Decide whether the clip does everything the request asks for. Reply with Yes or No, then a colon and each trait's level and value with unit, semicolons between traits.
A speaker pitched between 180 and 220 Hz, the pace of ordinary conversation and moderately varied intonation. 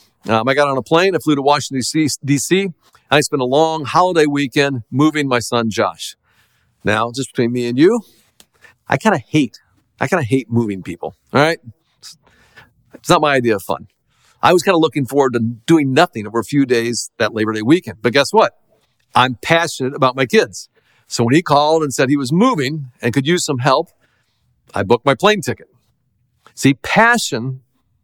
No: low, 135 Hz; average, 195 wpm; average, 4.1 semitones